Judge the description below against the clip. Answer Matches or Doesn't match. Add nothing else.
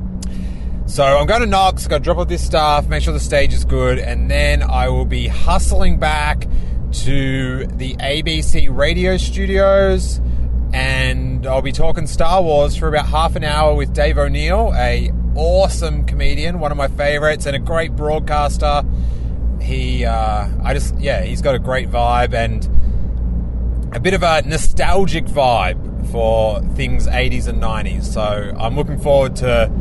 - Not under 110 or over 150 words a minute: Doesn't match